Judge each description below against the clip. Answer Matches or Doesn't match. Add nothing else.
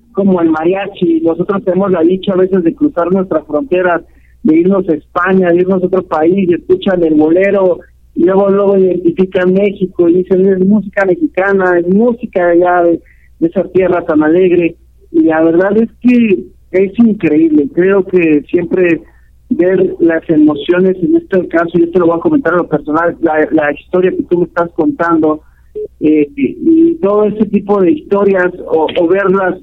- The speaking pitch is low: Doesn't match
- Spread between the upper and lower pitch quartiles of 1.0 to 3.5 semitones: Matches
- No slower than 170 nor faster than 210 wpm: Matches